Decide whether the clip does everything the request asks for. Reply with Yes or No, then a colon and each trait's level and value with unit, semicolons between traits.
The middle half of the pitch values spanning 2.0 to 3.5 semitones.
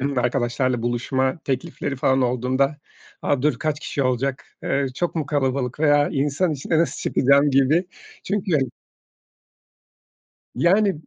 Yes: average, 2.8 semitones